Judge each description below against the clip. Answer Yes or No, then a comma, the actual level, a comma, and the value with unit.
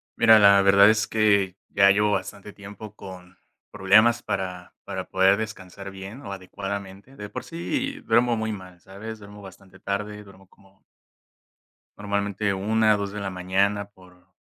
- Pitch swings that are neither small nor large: No, narrow, 1.6 semitones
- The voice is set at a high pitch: No, low, 100 Hz